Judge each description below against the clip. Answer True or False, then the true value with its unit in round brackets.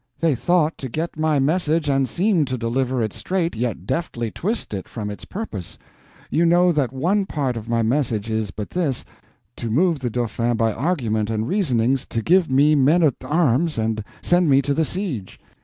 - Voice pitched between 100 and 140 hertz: True (135 Hz)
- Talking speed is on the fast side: False (190 wpm)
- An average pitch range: False (6.4 semitones)